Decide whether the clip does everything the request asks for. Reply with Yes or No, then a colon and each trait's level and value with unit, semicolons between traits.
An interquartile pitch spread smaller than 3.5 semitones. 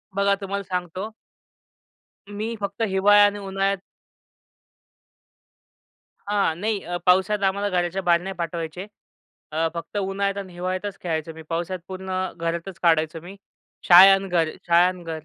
Yes: narrow, 2.6 semitones